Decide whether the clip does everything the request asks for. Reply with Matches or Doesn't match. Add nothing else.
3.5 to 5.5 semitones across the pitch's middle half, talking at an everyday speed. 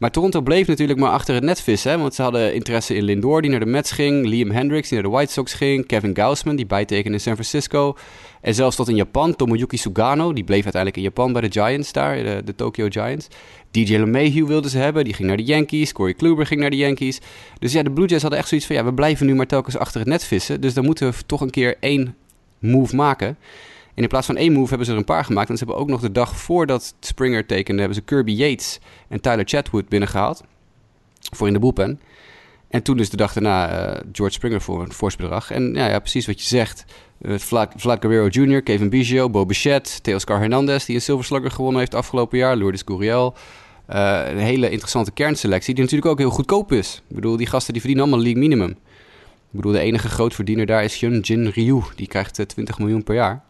Doesn't match